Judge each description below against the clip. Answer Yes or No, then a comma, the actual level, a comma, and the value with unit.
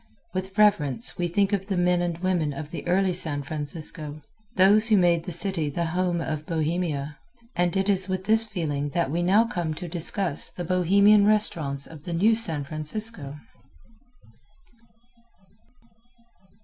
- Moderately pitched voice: Yes, medium, 175 Hz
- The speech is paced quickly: No, average, 155 wpm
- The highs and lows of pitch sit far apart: No, average, 3.8 semitones